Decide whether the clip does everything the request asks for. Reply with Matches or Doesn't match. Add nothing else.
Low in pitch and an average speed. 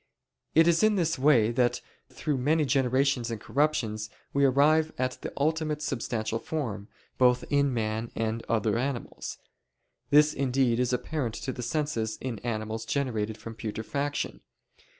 Matches